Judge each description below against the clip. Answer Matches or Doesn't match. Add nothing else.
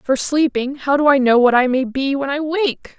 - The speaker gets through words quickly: Matches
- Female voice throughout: Matches